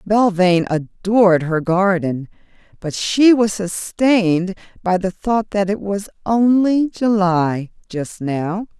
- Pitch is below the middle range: No, high, 195 Hz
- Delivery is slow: Yes, slow, 125 wpm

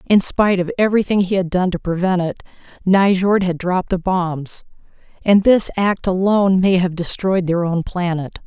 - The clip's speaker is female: Yes, female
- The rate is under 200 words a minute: Yes, average, 175 wpm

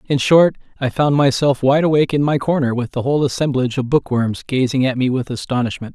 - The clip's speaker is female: No, male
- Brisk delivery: Yes, fast, 210 wpm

